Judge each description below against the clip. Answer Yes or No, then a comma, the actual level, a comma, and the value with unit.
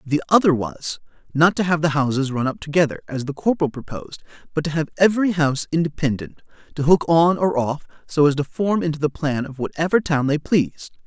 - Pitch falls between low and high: Yes, medium, 150 Hz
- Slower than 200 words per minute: No, fast, 205 wpm